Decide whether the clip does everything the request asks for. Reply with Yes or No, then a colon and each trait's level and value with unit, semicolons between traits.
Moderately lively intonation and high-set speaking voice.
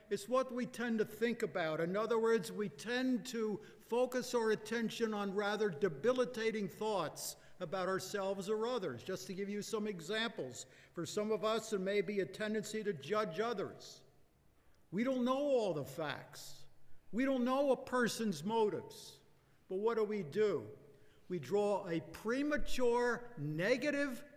Yes: average, 3.2 semitones; high, 215 Hz